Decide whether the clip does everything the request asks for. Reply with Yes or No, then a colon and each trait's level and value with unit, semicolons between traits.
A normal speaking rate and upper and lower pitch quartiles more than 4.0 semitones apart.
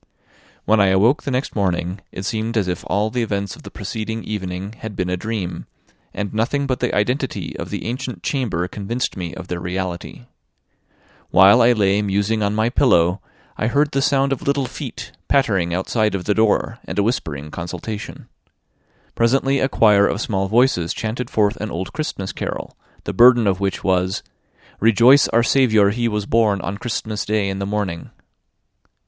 No: average, 180 wpm; average, 3.7 semitones